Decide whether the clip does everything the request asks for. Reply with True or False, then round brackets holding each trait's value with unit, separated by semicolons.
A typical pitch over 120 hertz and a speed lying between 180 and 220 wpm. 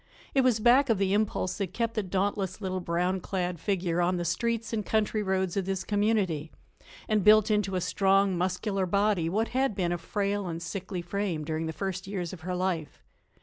True (190 Hz; 200 wpm)